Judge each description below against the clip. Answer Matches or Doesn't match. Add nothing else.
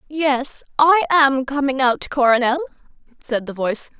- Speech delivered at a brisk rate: Doesn't match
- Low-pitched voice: Doesn't match